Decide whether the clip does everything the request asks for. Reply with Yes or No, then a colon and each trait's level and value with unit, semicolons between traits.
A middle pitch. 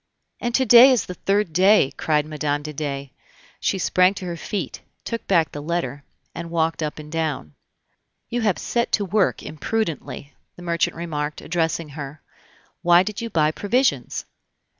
Yes: medium, 165 Hz